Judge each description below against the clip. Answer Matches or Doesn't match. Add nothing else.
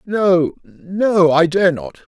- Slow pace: Matches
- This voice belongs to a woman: Doesn't match